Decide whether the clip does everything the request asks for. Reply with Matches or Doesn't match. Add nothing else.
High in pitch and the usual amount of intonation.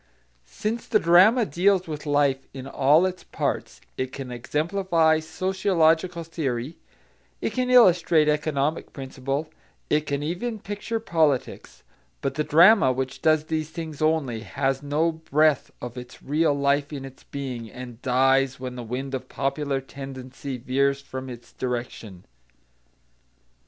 Doesn't match